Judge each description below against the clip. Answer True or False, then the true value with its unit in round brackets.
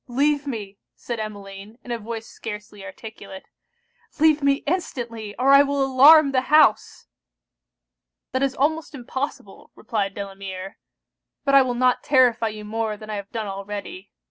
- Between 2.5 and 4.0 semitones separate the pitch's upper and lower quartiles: False (4.9 semitones)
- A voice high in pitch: True (235 Hz)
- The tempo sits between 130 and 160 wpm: True (150 wpm)